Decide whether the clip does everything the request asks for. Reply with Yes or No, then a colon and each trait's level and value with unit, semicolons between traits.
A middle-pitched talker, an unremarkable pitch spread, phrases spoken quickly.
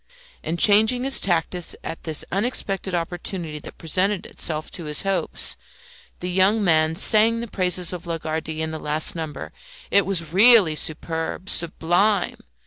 No: medium, 175 Hz; average, 3.7 semitones; average, 145 wpm